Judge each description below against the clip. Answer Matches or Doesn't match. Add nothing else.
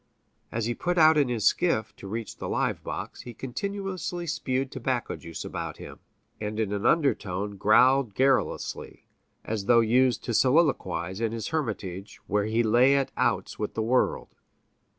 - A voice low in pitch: Matches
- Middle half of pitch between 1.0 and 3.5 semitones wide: Doesn't match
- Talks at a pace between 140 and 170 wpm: Matches